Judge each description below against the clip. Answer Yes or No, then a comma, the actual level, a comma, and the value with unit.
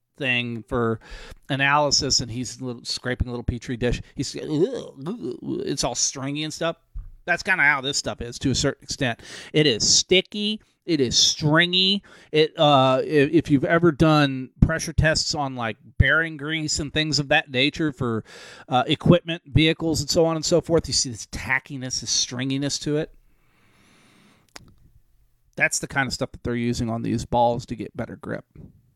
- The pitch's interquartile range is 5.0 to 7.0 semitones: No, average, 4.5 semitones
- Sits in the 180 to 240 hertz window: No, medium, 140 Hz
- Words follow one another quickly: No, average, 175 wpm